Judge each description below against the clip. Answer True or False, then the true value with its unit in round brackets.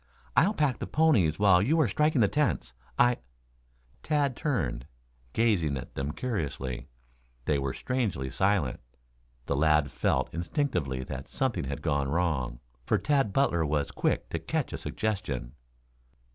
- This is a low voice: True (85 Hz)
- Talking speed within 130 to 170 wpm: True (145 wpm)